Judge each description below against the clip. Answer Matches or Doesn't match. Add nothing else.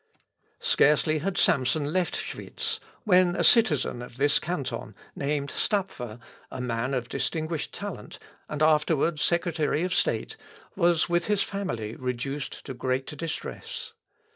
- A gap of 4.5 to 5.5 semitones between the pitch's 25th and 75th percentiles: Matches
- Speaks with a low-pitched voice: Doesn't match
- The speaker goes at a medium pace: Doesn't match